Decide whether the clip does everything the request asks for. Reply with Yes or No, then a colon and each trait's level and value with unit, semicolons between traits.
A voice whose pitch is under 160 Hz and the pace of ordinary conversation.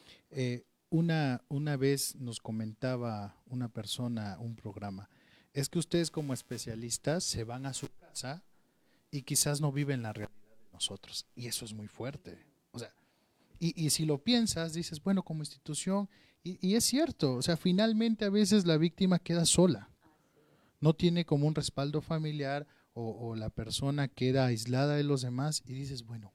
Yes: medium, 140 Hz; average, 170 wpm